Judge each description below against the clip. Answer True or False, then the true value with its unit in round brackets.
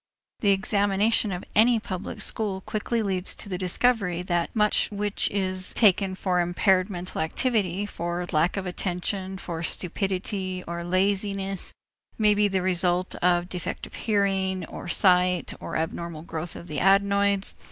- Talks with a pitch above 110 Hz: True (190 Hz)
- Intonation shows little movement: True (2.2 semitones)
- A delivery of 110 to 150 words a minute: True (145 wpm)